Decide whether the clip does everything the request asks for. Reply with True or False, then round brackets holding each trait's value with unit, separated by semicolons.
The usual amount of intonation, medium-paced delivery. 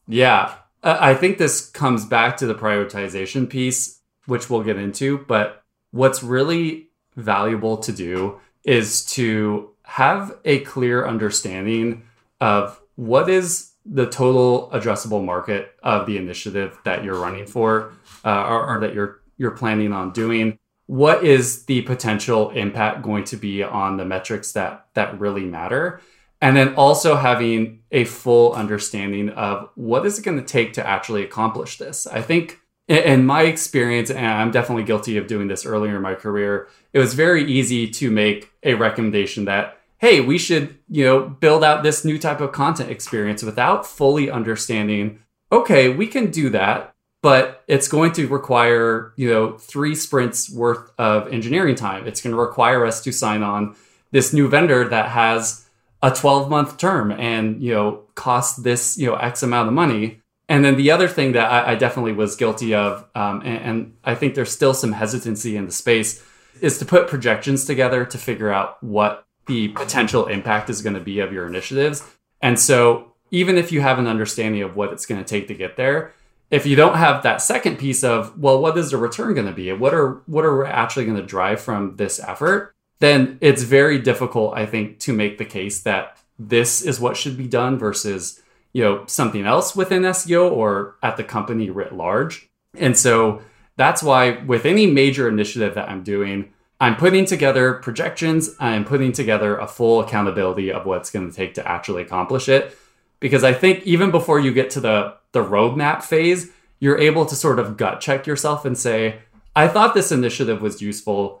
True (4.4 semitones; 185 wpm)